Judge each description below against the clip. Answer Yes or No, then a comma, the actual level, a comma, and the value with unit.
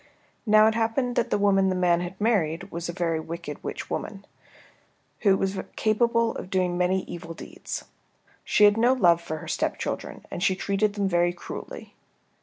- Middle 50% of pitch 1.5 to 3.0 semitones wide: No, average, 3.6 semitones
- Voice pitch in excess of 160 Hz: Yes, high, 190 Hz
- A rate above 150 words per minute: Yes, average, 180 wpm